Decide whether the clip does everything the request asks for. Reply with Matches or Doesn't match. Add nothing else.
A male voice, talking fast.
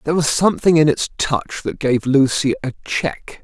Doesn't match